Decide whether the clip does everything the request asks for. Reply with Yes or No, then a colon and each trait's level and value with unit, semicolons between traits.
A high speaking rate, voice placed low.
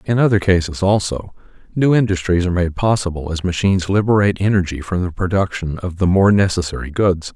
No: average, 170 wpm; very low, 95 Hz